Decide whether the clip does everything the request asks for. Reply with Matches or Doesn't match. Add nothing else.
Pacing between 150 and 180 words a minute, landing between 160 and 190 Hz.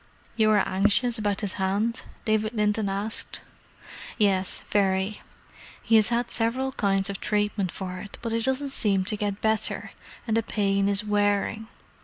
Doesn't match